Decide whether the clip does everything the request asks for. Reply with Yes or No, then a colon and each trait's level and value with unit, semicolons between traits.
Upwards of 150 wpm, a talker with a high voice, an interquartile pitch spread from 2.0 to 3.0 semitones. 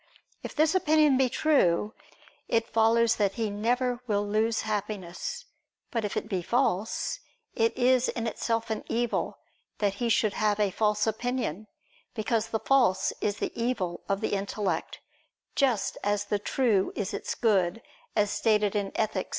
Yes: average, 160 wpm; high, 220 Hz; average, 2.7 semitones